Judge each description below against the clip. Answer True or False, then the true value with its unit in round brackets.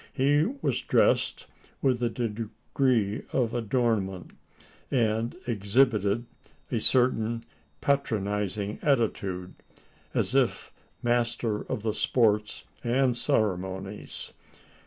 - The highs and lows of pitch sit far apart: False (3.0 semitones)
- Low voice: True (115 Hz)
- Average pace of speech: False (90 wpm)